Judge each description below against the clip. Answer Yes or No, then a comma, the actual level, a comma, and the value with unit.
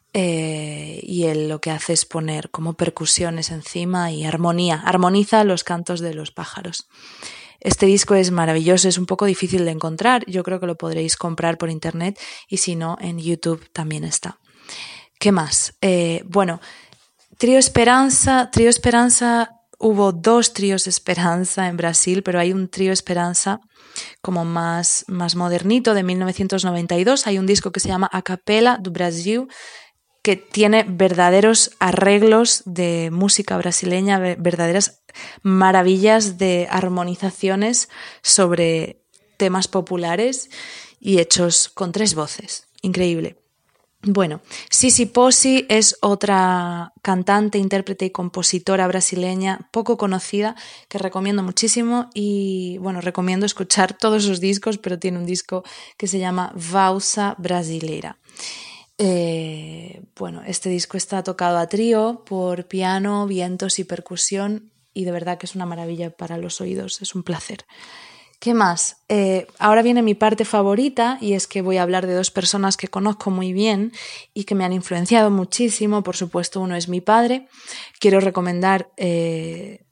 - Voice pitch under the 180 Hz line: No, high, 190 Hz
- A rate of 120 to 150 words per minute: Yes, average, 145 wpm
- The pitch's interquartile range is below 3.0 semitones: Yes, narrow, 2.6 semitones